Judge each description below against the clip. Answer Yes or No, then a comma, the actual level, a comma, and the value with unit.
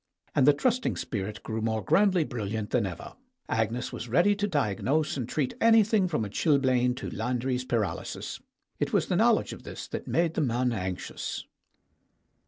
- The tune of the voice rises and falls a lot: Yes, wide, 6.3 semitones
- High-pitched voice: No, low, 125 Hz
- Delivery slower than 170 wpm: No, average, 175 wpm